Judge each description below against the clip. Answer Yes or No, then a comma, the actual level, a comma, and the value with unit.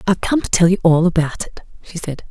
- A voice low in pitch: No, medium, 175 Hz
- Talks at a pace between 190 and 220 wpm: No, fast, 260 wpm